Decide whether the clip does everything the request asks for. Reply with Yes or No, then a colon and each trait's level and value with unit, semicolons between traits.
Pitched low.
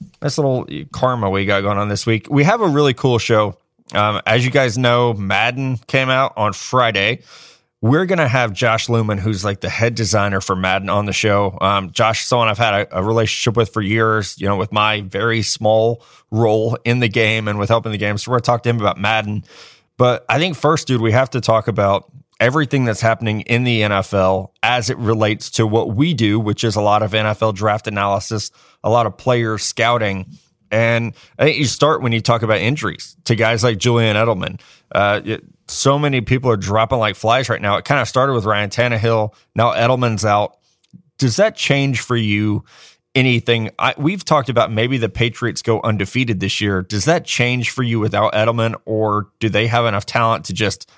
Yes: low, 115 Hz